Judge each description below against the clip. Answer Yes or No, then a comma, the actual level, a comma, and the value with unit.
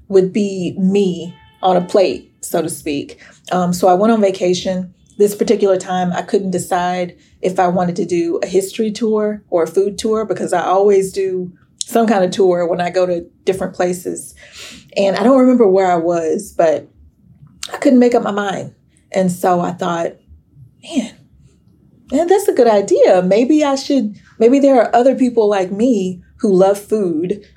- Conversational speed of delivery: Yes, average, 185 wpm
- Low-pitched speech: No, high, 190 Hz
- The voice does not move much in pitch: No, average, 3.2 semitones